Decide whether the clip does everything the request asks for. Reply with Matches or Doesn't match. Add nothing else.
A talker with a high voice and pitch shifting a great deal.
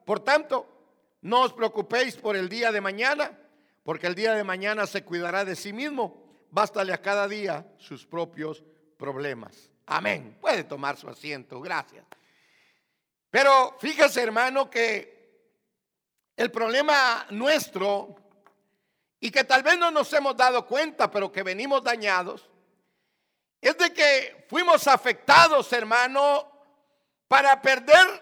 Matches